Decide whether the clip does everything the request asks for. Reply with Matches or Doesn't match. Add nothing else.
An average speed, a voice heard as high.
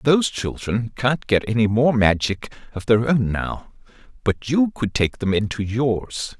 Doesn't match